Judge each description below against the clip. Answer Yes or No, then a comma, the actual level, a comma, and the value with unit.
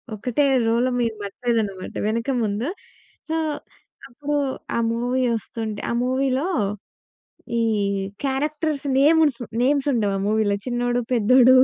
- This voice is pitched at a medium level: No, high, 245 Hz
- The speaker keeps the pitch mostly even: No, average, 3.5 semitones